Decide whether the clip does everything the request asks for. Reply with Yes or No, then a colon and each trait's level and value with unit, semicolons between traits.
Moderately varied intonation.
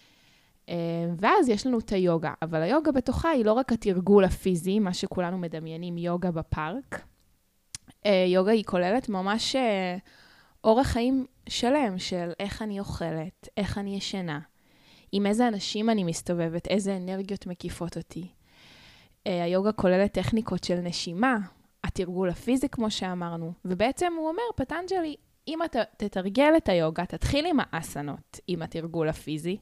Yes: average, 4.5 semitones